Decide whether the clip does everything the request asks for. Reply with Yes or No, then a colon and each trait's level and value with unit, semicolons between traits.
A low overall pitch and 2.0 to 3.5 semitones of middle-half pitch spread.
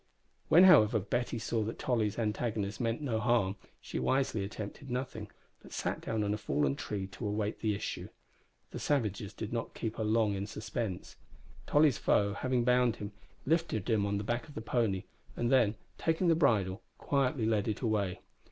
Yes: low, 110 Hz; average, 3.2 semitones